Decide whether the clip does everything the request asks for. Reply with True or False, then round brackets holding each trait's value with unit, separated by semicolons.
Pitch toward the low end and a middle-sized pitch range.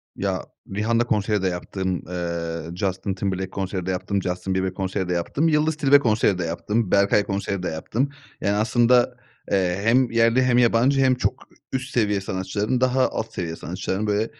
True (100 Hz; 4.2 semitones)